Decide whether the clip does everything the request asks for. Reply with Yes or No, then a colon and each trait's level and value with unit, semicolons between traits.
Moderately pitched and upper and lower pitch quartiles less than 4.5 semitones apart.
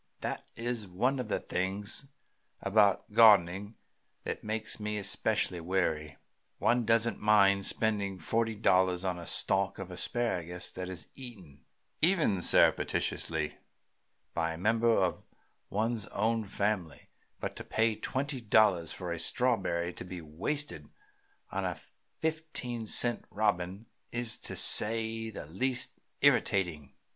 No: low, 105 Hz; average, 4.0 semitones